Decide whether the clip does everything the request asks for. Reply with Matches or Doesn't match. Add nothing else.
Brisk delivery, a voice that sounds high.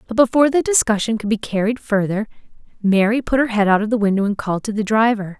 Matches